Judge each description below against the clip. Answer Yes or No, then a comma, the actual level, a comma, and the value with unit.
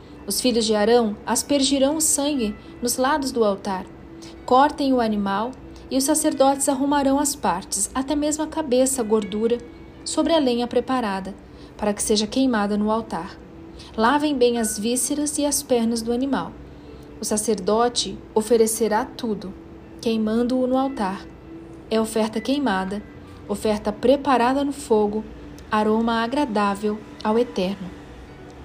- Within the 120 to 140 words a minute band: Yes, average, 130 wpm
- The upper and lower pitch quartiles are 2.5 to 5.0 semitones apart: Yes, average, 3.9 semitones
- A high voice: Yes, high, 235 Hz